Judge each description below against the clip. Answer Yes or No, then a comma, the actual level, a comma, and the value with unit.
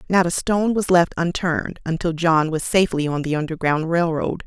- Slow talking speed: No, average, 200 wpm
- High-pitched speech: No, medium, 165 Hz